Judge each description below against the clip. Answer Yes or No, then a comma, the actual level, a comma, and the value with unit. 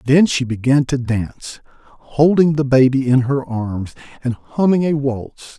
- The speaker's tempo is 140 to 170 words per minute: Yes, average, 160 wpm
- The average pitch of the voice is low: Yes, low, 130 Hz